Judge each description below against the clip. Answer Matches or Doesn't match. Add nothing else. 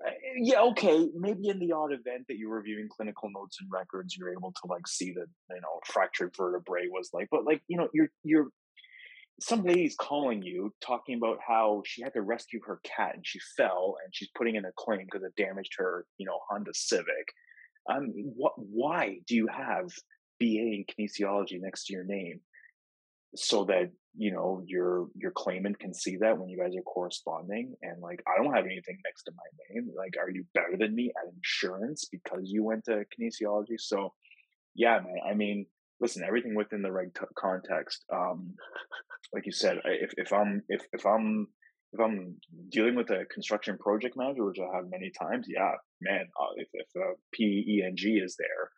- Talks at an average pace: Matches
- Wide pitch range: Matches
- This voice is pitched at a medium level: Doesn't match